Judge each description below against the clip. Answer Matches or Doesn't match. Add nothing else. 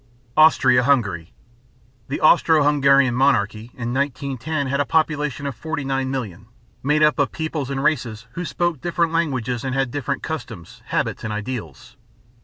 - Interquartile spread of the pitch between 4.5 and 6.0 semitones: Doesn't match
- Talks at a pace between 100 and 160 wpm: Matches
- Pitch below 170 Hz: Matches